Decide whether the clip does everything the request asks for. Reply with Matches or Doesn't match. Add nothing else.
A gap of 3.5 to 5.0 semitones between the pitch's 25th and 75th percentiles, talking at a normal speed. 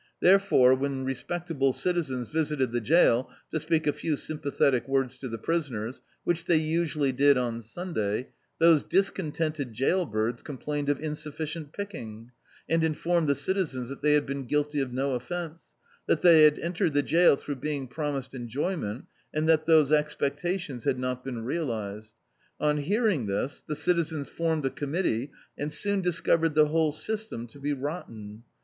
Matches